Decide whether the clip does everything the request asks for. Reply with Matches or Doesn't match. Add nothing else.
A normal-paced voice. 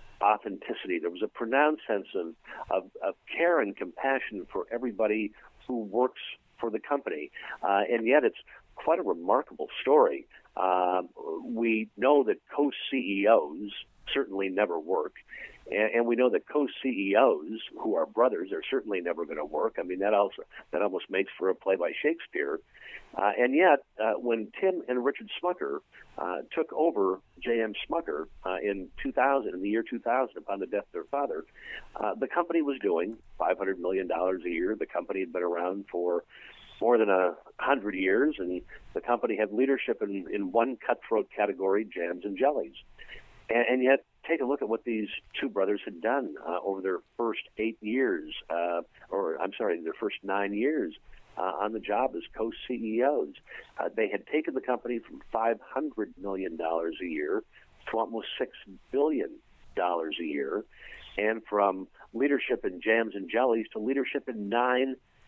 Matches